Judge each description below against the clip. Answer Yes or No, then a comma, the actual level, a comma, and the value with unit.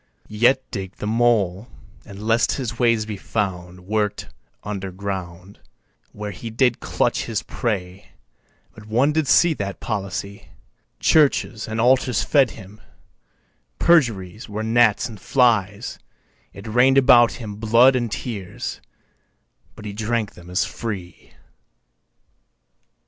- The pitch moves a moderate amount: Yes, average, 3.3 semitones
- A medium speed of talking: No, slow, 125 wpm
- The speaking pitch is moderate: No, low, 110 Hz